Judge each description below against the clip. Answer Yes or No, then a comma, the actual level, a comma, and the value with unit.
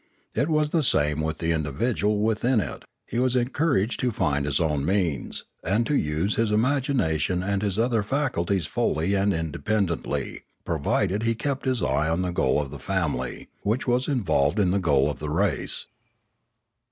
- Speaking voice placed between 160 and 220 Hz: No, low, 100 Hz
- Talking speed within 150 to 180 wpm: Yes, average, 175 wpm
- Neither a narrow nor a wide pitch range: No, wide, 7.0 semitones